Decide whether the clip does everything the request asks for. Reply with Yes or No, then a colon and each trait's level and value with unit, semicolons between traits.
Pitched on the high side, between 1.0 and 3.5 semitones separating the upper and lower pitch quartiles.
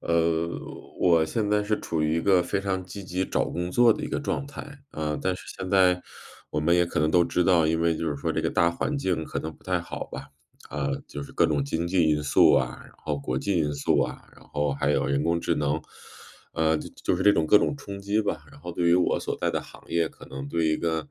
No: very low, 85 Hz; average, 3.2 semitones